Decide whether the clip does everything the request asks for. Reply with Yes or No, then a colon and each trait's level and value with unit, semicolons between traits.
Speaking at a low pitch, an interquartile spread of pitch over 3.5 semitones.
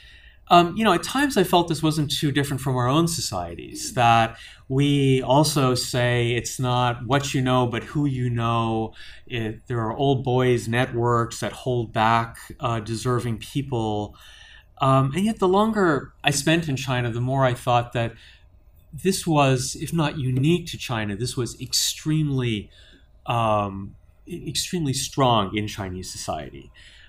Yes: low, 125 Hz; average, 4.0 semitones